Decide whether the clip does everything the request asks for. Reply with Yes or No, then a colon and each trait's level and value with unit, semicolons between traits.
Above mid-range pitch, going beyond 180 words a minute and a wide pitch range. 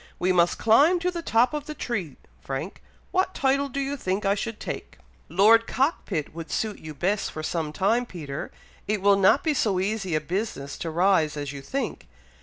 Yes: high, 200 Hz; average, 200 wpm; wide, 6.8 semitones